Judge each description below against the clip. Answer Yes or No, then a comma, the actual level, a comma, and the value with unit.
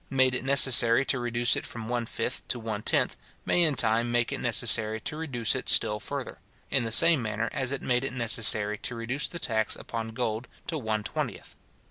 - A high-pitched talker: No, low, 120 Hz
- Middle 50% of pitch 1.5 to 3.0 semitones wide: Yes, average, 2.7 semitones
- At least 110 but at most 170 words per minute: No, fast, 205 wpm